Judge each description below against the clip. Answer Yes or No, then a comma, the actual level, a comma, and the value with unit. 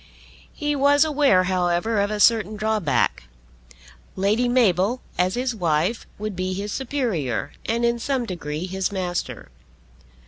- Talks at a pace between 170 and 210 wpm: No, slow, 135 wpm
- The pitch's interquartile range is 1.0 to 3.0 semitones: No, average, 4.7 semitones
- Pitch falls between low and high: No, high, 210 Hz